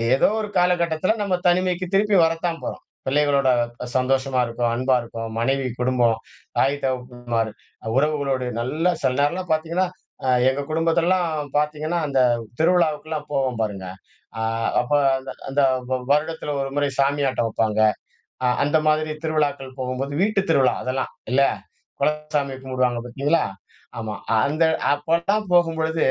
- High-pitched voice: No, medium, 145 Hz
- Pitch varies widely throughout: No, average, 4.0 semitones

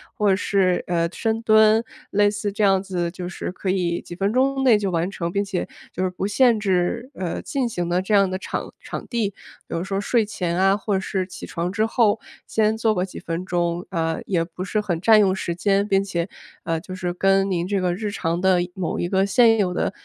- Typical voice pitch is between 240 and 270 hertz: No, high, 195 Hz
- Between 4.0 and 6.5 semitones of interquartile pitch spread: No, average, 2.8 semitones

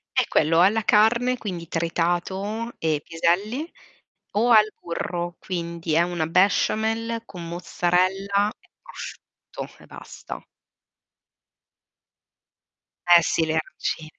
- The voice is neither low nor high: Yes, medium, 180 Hz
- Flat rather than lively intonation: No, average, 4.2 semitones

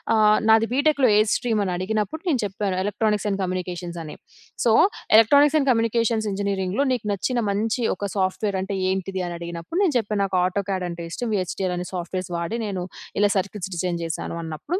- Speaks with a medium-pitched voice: No, high, 200 Hz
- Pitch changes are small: No, average, 3.6 semitones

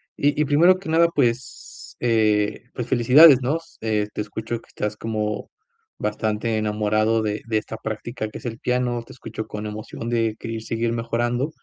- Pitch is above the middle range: No, low, 115 Hz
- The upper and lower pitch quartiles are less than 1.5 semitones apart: No, narrow, 2.4 semitones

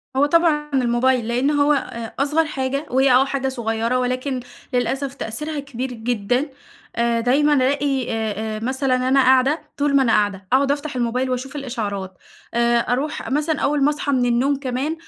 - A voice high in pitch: Yes, very high, 260 Hz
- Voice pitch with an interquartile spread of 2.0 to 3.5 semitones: Yes, average, 2.9 semitones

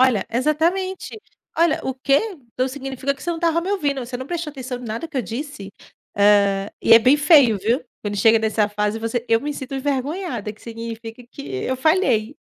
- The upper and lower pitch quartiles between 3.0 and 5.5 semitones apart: Yes, average, 4.9 semitones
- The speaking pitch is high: Yes, very high, 260 Hz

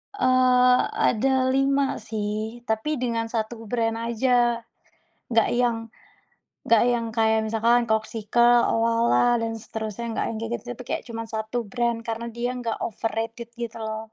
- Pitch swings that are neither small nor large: No, narrow, 1.5 semitones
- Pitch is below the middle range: No, high, 230 Hz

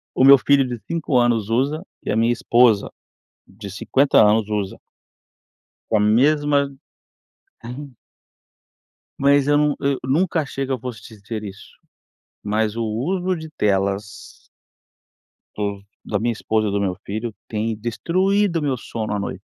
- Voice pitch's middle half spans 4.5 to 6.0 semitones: Yes, average, 5.0 semitones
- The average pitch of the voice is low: Yes, low, 120 Hz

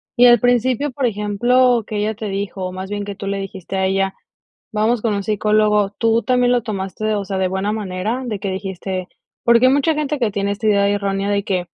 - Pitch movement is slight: No, average, 3.3 semitones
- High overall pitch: Yes, high, 205 Hz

